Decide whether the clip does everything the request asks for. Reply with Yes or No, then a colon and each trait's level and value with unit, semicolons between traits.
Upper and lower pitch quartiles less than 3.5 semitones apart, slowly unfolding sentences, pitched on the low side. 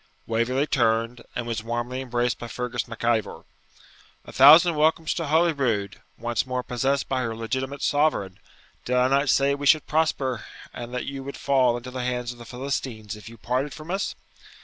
No: average, 2.9 semitones; average, 185 wpm; low, 125 Hz